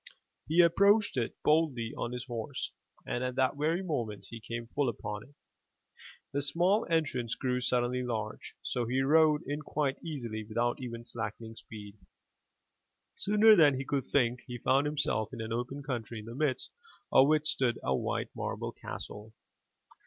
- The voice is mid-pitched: No, low, 125 Hz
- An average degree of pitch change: Yes, average, 4.2 semitones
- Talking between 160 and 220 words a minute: Yes, average, 165 wpm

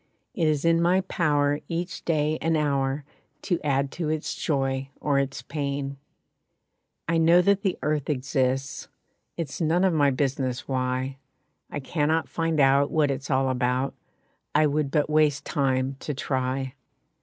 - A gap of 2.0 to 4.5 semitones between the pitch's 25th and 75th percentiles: Yes, average, 2.8 semitones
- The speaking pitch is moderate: Yes, medium, 145 Hz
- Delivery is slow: No, average, 155 wpm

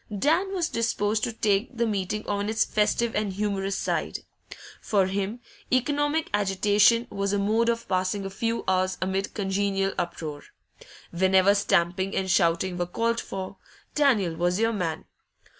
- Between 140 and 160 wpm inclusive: Yes, average, 150 wpm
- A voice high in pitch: Yes, high, 200 Hz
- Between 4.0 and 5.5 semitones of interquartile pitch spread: No, average, 3.3 semitones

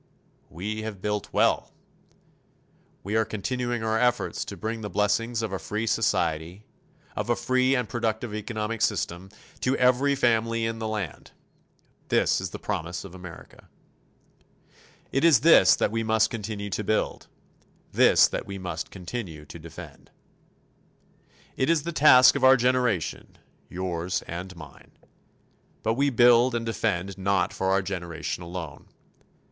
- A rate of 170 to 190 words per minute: No, average, 145 wpm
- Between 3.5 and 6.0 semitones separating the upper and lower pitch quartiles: Yes, average, 4.4 semitones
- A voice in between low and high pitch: No, low, 110 Hz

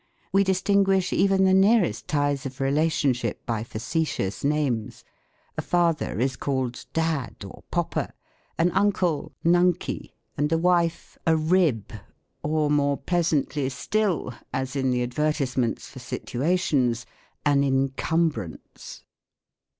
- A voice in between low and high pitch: Yes, medium, 150 Hz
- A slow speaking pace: Yes, slow, 125 wpm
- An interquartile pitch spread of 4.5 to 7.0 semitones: Yes, average, 5.0 semitones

